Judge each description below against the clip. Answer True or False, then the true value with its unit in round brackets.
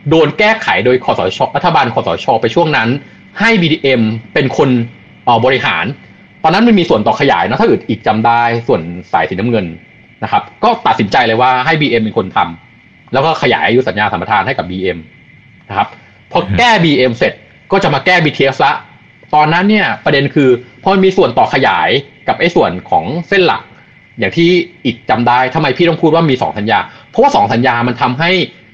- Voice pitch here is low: False (145 Hz)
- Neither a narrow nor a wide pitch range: False (6.1 semitones)